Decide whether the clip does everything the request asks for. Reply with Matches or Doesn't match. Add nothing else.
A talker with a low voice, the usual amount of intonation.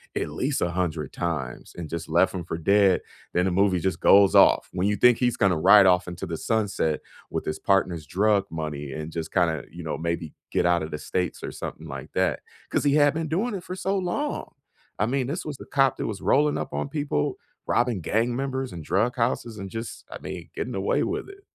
Doesn't match